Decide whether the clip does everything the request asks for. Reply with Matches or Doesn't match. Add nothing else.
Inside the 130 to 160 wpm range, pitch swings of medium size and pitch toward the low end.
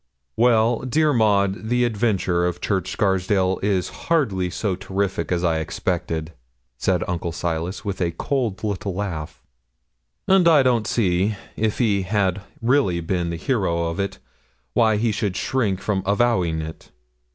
Matches